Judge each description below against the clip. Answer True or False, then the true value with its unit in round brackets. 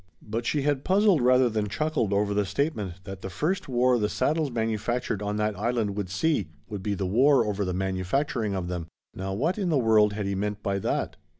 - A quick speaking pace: True (215 wpm)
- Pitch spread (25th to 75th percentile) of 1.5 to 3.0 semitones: False (4.8 semitones)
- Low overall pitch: True (105 Hz)